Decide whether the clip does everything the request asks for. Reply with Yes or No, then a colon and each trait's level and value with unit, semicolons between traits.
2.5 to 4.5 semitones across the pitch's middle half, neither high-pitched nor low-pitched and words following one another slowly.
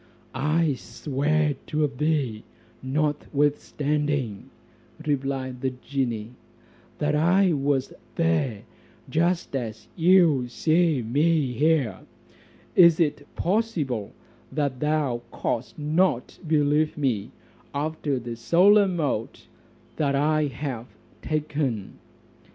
Yes: average, 3.4 semitones; medium, 145 Hz; slow, 90 wpm